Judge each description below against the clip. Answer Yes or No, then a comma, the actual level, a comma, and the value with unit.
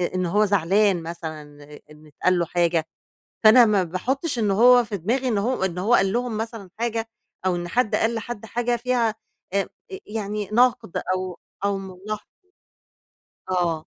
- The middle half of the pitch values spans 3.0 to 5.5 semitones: Yes, average, 4.2 semitones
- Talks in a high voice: Yes, high, 205 Hz